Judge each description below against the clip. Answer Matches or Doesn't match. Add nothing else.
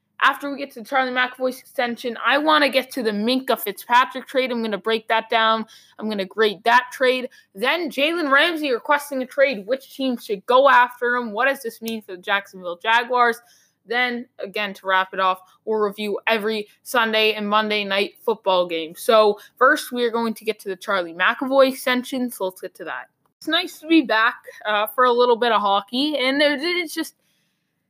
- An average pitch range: Matches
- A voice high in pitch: Matches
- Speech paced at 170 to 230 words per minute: Matches